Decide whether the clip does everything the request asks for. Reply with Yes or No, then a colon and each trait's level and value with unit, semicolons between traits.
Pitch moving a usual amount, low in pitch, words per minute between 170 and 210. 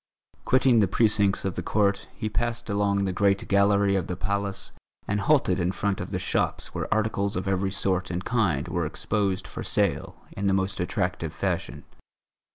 No: narrow, 1.7 semitones; low, 100 Hz; average, 180 wpm